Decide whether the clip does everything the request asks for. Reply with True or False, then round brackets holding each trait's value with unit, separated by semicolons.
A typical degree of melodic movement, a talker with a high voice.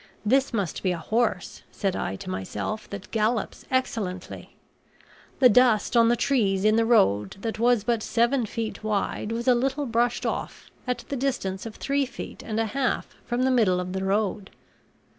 True (3.8 semitones; 225 Hz)